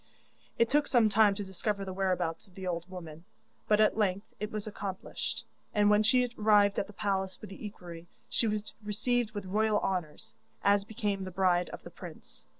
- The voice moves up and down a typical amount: No, narrow, 2.3 semitones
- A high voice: Yes, high, 200 Hz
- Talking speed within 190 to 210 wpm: Yes, average, 195 wpm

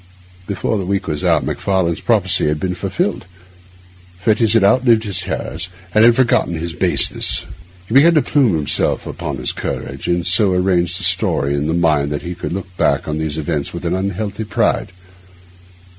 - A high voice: No, very low, 90 Hz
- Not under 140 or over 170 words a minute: No, average, 185 wpm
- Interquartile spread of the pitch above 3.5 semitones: Yes, average, 4.5 semitones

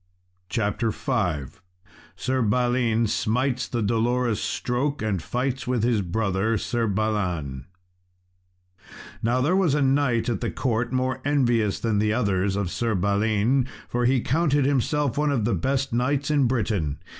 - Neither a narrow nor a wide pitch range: Yes, average, 3.7 semitones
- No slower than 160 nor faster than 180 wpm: No, average, 145 wpm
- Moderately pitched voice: No, low, 120 Hz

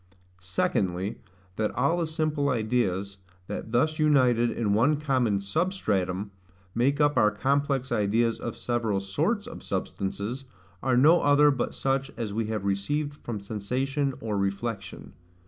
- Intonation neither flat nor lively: No, wide, 6.0 semitones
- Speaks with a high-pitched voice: No, low, 120 Hz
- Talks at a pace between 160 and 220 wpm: No, average, 140 wpm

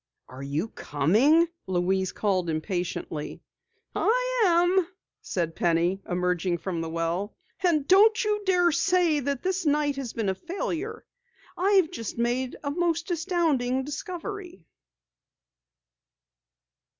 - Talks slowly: Yes, slow, 115 wpm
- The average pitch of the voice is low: No, very high, 285 Hz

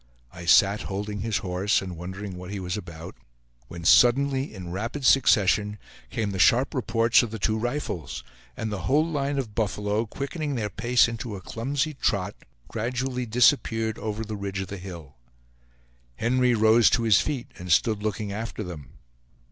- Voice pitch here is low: Yes, low, 110 Hz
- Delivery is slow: No, average, 170 wpm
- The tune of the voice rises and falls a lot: No, average, 3.9 semitones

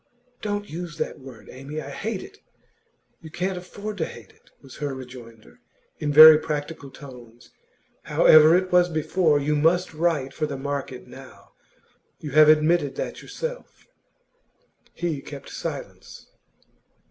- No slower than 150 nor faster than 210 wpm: No, average, 140 wpm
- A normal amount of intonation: Yes, average, 4.1 semitones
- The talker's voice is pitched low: No, medium, 155 Hz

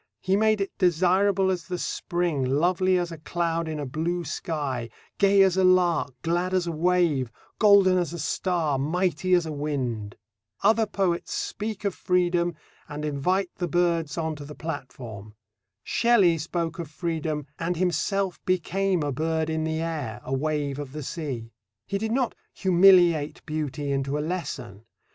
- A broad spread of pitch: No, average, 3.6 semitones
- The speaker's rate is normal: Yes, average, 165 wpm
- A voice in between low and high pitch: Yes, medium, 170 Hz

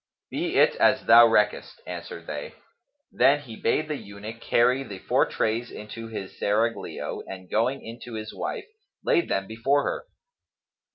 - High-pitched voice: No, low, 115 Hz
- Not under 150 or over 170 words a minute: Yes, average, 160 wpm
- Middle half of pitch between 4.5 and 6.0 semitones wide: No, average, 2.9 semitones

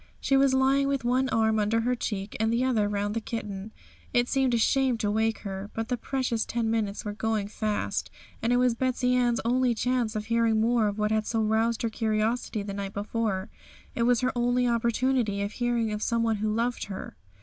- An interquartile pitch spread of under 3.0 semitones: Yes, narrow, 2.5 semitones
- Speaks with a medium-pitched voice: No, high, 230 Hz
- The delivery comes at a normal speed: No, fast, 215 wpm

